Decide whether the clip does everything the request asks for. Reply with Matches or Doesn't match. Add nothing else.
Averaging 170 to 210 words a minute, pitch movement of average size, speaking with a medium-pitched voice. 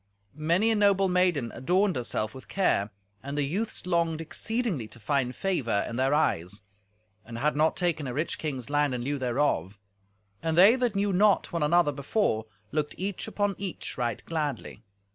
Doesn't match